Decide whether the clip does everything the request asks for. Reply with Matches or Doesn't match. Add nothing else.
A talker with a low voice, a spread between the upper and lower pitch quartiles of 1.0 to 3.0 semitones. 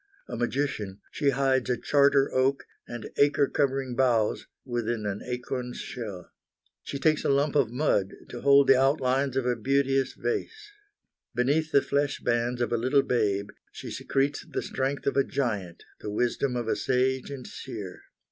Matches